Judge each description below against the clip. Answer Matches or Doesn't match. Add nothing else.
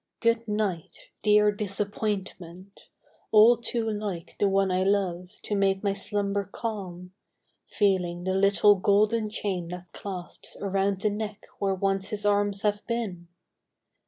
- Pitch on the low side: Doesn't match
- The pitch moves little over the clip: Matches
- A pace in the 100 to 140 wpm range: Matches